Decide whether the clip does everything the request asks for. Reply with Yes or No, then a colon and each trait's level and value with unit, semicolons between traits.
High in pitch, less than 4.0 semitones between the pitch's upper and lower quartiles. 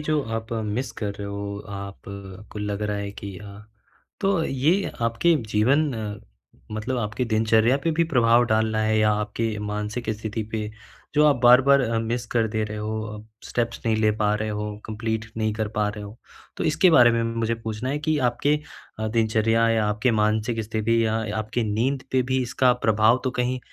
No: low, 110 Hz; narrow, 2.5 semitones